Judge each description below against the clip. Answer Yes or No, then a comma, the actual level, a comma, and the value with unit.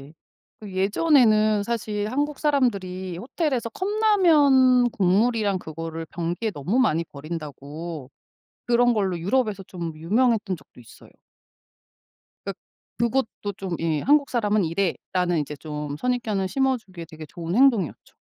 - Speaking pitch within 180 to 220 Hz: Yes, high, 205 Hz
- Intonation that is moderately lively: No, wide, 6.6 semitones